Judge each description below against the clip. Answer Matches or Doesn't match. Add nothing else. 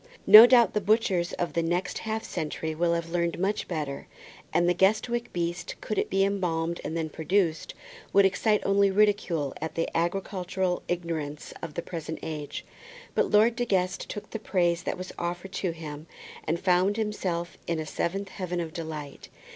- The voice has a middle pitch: Matches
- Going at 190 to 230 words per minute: Doesn't match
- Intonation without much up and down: Doesn't match